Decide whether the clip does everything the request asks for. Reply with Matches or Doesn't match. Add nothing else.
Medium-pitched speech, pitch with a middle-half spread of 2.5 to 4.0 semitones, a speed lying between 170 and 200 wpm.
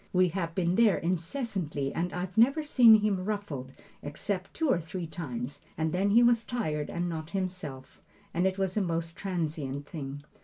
Doesn't match